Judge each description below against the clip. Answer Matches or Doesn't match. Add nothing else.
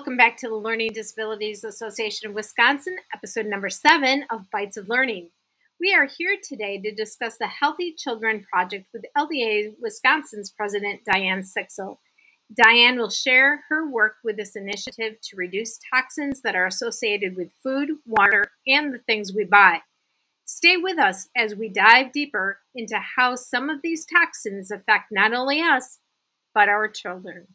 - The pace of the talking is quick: Doesn't match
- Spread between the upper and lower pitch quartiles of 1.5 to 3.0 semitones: Doesn't match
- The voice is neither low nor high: Doesn't match